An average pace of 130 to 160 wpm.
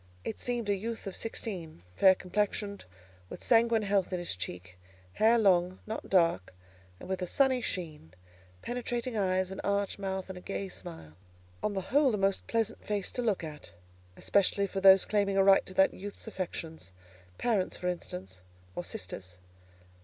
No: average, 170 wpm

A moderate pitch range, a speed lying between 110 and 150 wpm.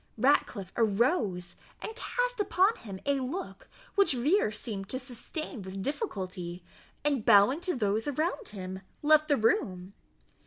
No: wide, 7.8 semitones; average, 140 wpm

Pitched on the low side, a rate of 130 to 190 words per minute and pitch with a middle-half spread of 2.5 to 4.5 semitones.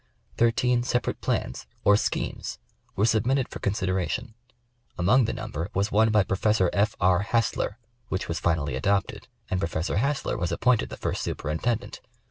Yes: low, 105 Hz; average, 150 wpm; average, 3.9 semitones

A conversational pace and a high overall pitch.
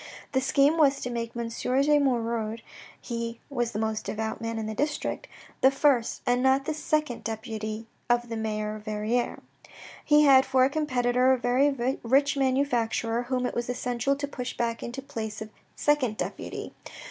Yes: average, 180 wpm; high, 245 Hz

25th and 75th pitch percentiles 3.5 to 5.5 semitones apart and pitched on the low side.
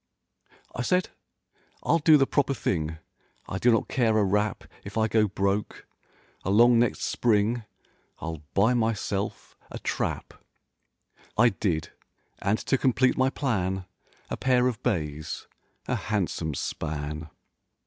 Yes: average, 4.5 semitones; low, 105 Hz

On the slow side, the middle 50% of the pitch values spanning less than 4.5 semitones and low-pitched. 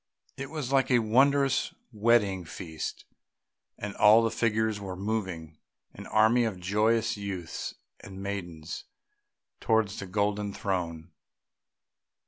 Yes: slow, 115 wpm; average, 3.3 semitones; low, 105 Hz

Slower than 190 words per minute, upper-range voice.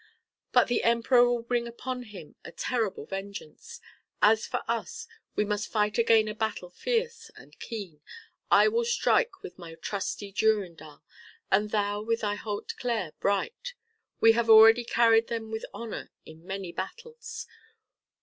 Yes: average, 150 wpm; high, 225 Hz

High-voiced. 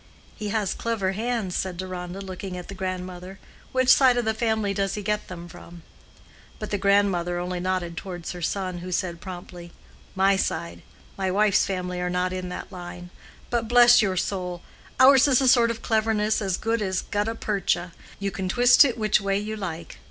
Yes: high, 195 Hz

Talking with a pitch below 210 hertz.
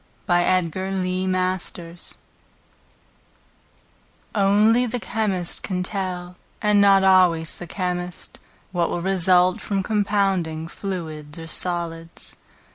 Yes: medium, 185 Hz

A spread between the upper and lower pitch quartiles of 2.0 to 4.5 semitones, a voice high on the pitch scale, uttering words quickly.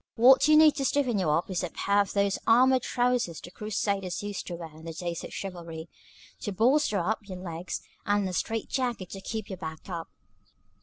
No: average, 5.0 semitones; high, 200 Hz; fast, 210 wpm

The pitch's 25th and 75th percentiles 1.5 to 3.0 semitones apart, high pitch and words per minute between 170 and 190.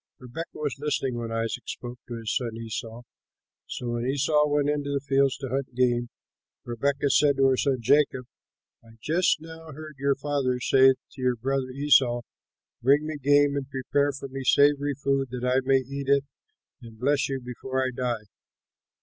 No: narrow, 2.4 semitones; low, 135 Hz; average, 180 wpm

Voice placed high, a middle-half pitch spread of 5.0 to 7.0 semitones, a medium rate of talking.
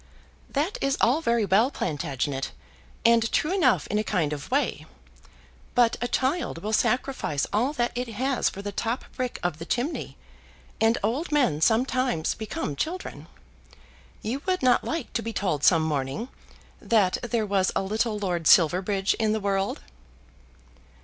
Yes: high, 220 Hz; wide, 5.4 semitones; average, 155 wpm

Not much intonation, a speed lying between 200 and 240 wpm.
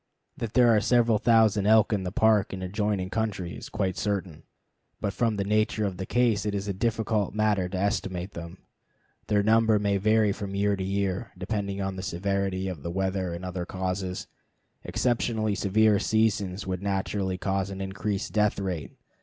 No: narrow, 2.3 semitones; average, 180 wpm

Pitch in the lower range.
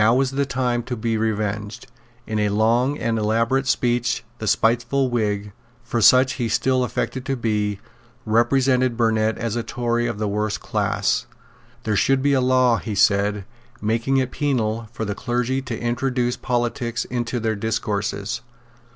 Yes: low, 120 Hz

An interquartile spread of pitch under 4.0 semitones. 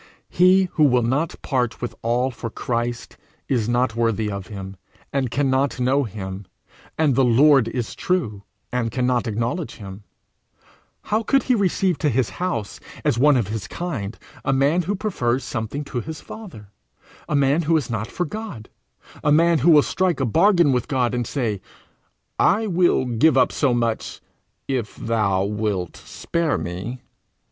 No: wide, 5.6 semitones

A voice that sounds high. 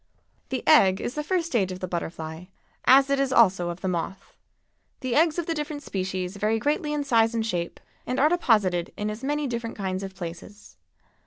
Yes: high, 225 Hz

